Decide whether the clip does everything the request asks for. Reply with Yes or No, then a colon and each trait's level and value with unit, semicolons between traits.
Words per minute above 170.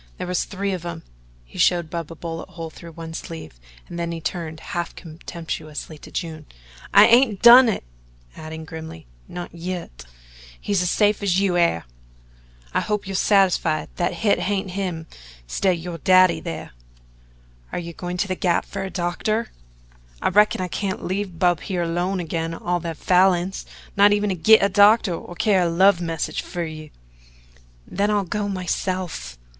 Yes: average, 180 wpm